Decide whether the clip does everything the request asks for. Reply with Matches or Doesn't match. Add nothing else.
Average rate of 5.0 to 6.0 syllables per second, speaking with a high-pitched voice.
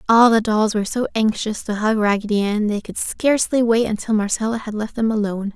Matches